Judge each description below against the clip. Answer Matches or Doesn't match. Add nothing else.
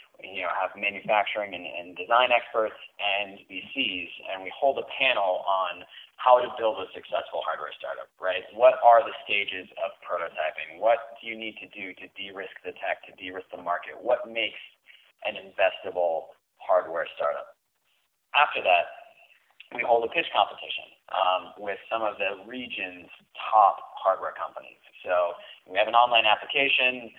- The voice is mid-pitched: Doesn't match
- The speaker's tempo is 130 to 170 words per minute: Matches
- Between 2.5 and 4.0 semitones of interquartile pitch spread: Doesn't match